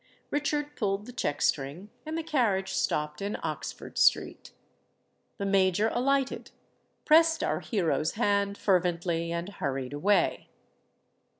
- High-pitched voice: Yes, high, 200 Hz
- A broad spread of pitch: Yes, wide, 6.6 semitones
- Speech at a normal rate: No, slow, 110 wpm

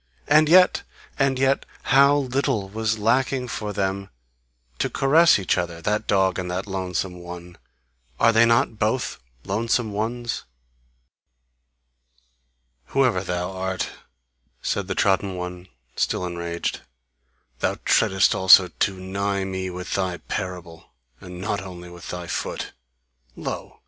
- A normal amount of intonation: Yes, average, 4.3 semitones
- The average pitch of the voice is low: Yes, very low, 95 Hz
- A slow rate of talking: Yes, slow, 130 wpm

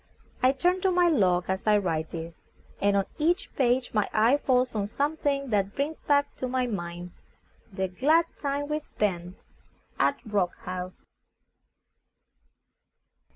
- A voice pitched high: Yes, high, 235 Hz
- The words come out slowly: No, average, 150 wpm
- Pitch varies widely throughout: Yes, wide, 7.2 semitones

